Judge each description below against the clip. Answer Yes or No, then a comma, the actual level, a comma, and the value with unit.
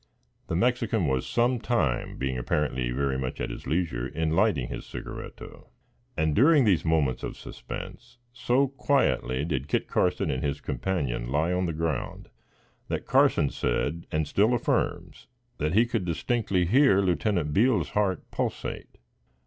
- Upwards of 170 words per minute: No, average, 150 wpm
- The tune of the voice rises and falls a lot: Yes, wide, 7.7 semitones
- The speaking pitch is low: Yes, very low, 85 Hz